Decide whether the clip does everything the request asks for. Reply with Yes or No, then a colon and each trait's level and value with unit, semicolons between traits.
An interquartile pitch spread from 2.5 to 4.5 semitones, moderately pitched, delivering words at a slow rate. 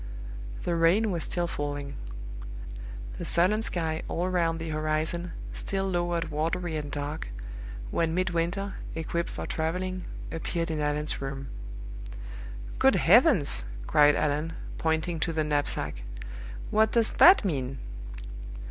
Yes: average, 2.8 semitones; medium, 165 Hz; slow, 120 wpm